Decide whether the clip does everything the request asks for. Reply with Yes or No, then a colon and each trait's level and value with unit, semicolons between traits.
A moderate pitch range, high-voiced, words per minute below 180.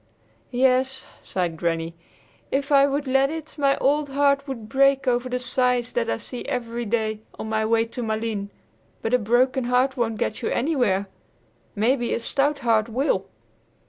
Yes: average, 3.6 semitones; very high, 250 Hz; average, 170 wpm